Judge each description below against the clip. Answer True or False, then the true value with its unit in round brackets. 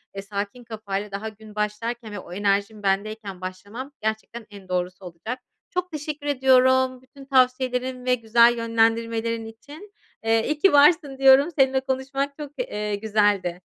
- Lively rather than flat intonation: False (4.2 semitones)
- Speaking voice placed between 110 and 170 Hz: False (230 Hz)